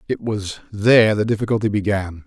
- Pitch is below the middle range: Yes, low, 105 Hz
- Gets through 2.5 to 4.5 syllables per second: No, 5.7 syllables/s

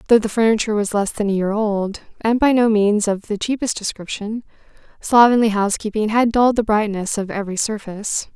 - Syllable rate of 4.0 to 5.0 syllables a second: No, 5.8 syllables/s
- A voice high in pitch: Yes, high, 215 Hz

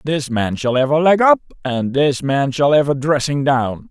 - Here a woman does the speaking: No, male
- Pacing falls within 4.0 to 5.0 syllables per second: Yes, 4.5 syllables/s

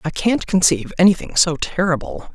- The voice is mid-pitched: Yes, medium, 175 Hz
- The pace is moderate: Yes, average, 155 wpm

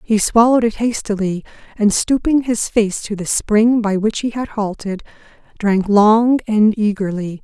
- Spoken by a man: No, female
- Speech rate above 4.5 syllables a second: No, 4.4 syllables/s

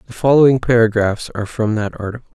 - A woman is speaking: No, male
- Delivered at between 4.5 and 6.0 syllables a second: No, 6.6 syllables/s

